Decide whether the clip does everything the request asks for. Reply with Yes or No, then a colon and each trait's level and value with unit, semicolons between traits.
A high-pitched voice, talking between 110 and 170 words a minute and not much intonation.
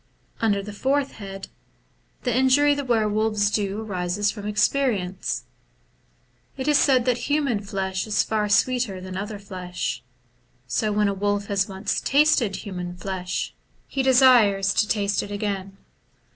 No: high, 205 Hz; average, 145 wpm; average, 4.0 semitones